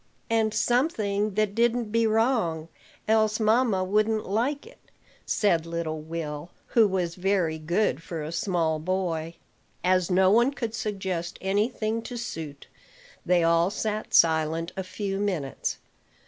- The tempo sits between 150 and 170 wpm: No, average, 140 wpm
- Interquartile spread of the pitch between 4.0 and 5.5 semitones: Yes, average, 4.6 semitones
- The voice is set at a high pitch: Yes, high, 195 Hz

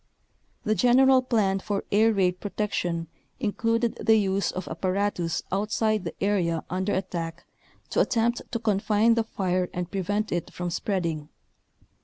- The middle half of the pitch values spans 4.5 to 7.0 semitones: No, average, 3.5 semitones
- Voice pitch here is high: Yes, high, 200 Hz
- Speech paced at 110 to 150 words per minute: Yes, average, 140 wpm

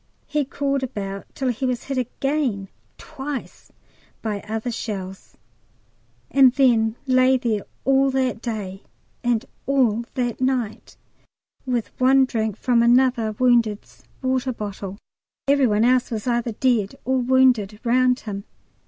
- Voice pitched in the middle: No, high, 245 Hz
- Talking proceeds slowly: Yes, slow, 130 wpm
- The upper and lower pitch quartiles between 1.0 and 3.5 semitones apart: Yes, average, 3.2 semitones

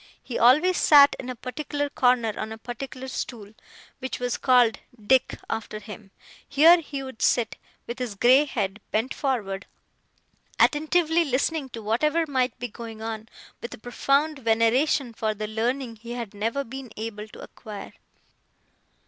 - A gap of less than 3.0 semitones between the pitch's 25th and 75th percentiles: No, average, 3.8 semitones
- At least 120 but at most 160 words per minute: Yes, average, 155 wpm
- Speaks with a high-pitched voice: Yes, high, 245 Hz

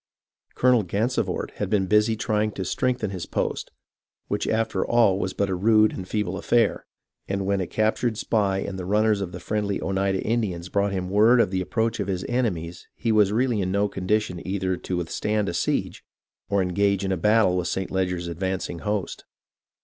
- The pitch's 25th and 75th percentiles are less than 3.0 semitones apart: Yes, narrow, 2.6 semitones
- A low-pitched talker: Yes, low, 100 Hz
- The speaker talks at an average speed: Yes, average, 190 wpm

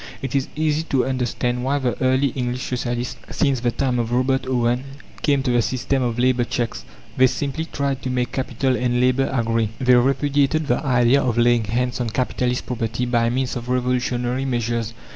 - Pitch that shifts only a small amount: Yes, narrow, 1.7 semitones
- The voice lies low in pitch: Yes, low, 125 Hz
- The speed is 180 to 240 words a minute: Yes, average, 185 wpm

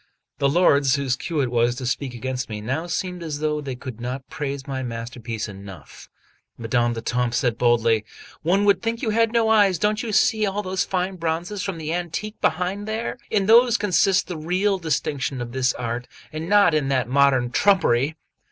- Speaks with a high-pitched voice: No, medium, 150 Hz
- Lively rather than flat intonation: Yes, wide, 7.5 semitones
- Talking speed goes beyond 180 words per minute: Yes, average, 190 wpm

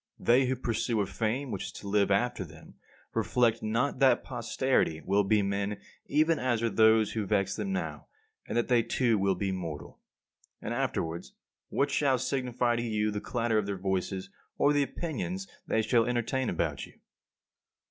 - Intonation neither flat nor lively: Yes, average, 4.1 semitones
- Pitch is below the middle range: Yes, low, 115 Hz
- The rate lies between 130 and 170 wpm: No, average, 180 wpm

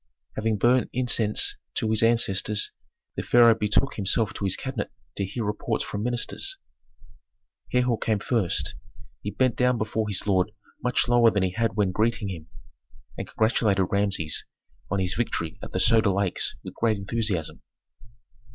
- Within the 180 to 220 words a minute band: No, average, 155 wpm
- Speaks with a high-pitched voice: No, low, 110 Hz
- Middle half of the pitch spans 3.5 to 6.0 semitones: No, average, 3.0 semitones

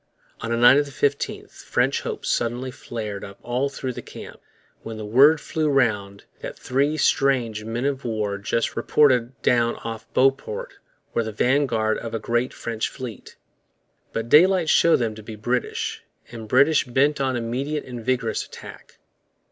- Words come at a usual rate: Yes, average, 165 wpm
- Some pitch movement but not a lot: Yes, average, 3.4 semitones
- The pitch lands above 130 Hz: No, low, 120 Hz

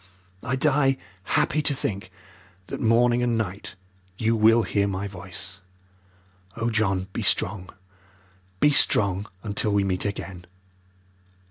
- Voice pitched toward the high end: No, low, 105 Hz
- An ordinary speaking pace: No, slow, 125 wpm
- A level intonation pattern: No, average, 3.5 semitones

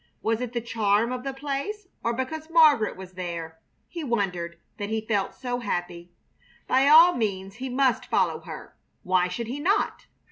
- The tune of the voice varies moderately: No, wide, 6.2 semitones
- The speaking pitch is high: Yes, high, 235 Hz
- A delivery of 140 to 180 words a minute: Yes, average, 175 wpm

